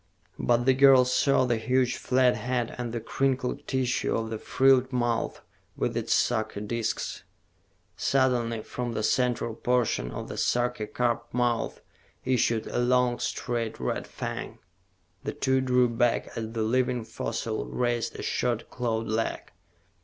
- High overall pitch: No, low, 120 Hz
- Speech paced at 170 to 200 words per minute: No, average, 145 wpm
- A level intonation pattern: Yes, narrow, 1.7 semitones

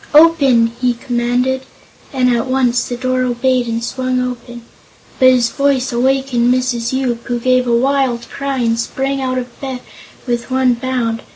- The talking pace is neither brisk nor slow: Yes, average, 165 wpm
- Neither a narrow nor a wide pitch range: No, narrow, 1.6 semitones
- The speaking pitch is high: Yes, very high, 250 Hz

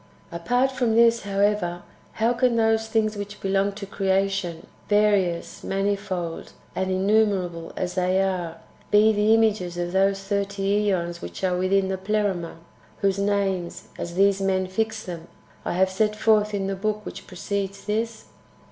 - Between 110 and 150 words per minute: No, average, 160 wpm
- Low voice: No, high, 195 Hz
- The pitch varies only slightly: Yes, narrow, 2.2 semitones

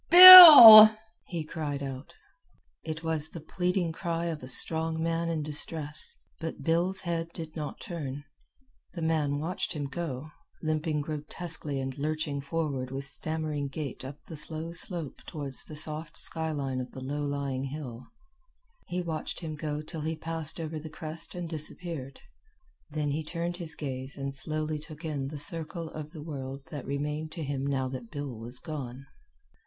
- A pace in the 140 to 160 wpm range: No, average, 170 wpm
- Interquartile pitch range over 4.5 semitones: No, narrow, 2.6 semitones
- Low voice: No, medium, 155 Hz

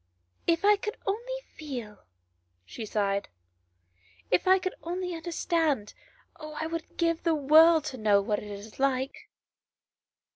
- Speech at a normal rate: Yes, average, 150 wpm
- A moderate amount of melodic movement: No, wide, 8.2 semitones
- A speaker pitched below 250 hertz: No, very high, 305 Hz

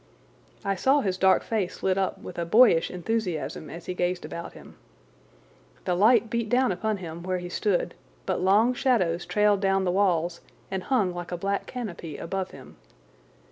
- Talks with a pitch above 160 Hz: Yes, high, 190 Hz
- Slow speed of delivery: No, average, 175 wpm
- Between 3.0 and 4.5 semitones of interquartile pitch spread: Yes, average, 3.4 semitones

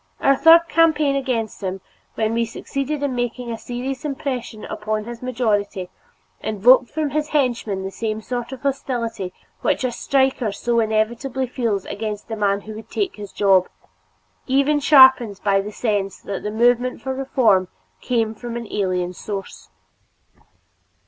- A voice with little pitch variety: No, average, 4.0 semitones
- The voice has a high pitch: Yes, high, 235 Hz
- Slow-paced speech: No, average, 155 wpm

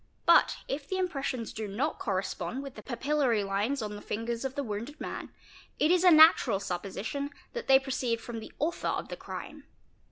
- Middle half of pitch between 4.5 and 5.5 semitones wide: Yes, average, 5.0 semitones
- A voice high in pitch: Yes, very high, 255 Hz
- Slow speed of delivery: No, average, 190 wpm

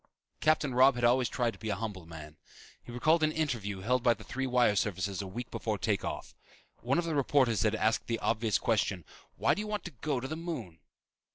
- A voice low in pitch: Yes, low, 120 Hz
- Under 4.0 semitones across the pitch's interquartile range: No, average, 4.8 semitones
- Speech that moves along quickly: Yes, fast, 225 wpm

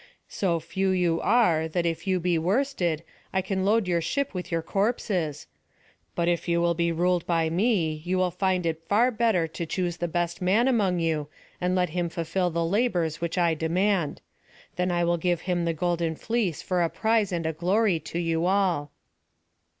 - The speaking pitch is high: No, medium, 175 Hz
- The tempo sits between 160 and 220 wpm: Yes, average, 195 wpm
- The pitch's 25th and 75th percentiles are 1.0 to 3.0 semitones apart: Yes, narrow, 2.4 semitones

